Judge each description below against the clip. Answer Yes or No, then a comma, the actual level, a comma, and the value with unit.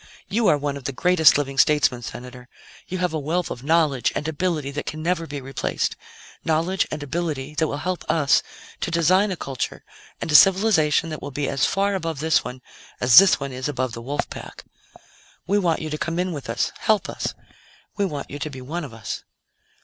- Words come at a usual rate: No, fast, 210 wpm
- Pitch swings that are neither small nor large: Yes, average, 4.0 semitones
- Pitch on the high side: No, medium, 150 Hz